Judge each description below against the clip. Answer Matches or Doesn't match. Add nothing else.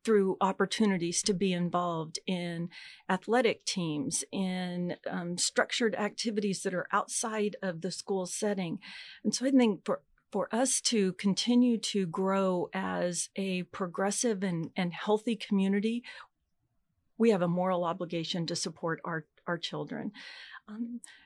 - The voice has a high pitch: Matches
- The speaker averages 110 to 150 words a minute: Matches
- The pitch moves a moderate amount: Matches